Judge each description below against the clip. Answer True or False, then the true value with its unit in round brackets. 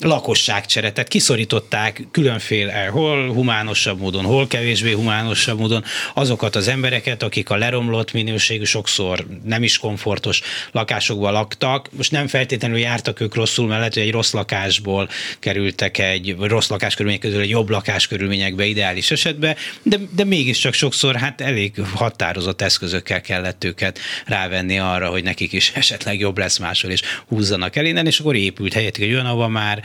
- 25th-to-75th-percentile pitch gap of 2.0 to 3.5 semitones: False (4.1 semitones)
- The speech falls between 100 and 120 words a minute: False (150 wpm)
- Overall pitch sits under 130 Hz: True (110 Hz)